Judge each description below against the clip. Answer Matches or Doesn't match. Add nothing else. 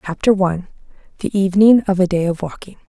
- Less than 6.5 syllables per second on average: Doesn't match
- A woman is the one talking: Matches